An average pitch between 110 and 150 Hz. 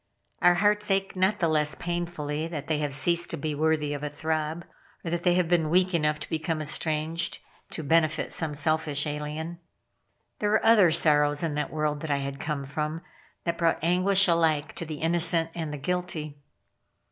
No: medium, 160 Hz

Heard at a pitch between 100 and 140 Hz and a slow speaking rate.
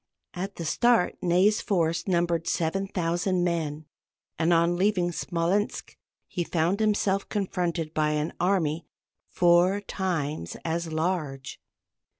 No: medium, 175 Hz; slow, 115 wpm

